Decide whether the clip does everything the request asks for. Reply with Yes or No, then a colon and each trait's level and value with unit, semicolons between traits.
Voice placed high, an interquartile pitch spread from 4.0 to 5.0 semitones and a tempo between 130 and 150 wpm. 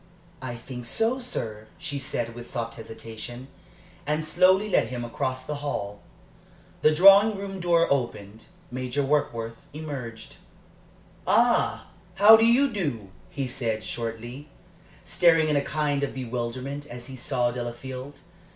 No: low, 130 Hz; average, 4.6 semitones; average, 140 wpm